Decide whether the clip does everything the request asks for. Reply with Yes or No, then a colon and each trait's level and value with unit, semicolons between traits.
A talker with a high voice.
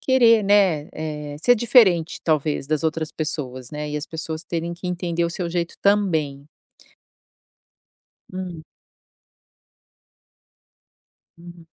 No: medium, 165 Hz